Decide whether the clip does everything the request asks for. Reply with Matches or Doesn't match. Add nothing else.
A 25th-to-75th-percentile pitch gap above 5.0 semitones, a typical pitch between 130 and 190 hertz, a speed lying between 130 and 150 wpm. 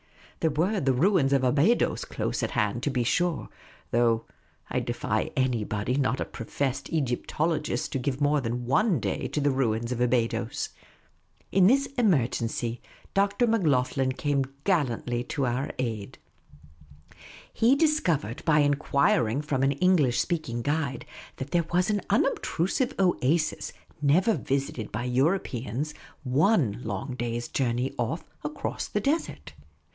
Matches